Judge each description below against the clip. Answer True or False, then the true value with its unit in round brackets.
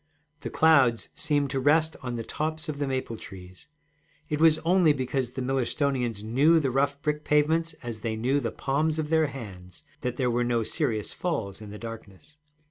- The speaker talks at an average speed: True (190 wpm)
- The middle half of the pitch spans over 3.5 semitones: True (4.6 semitones)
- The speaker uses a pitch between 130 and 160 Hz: True (135 Hz)